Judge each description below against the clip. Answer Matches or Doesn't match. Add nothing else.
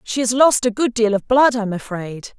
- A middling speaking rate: Doesn't match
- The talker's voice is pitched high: Matches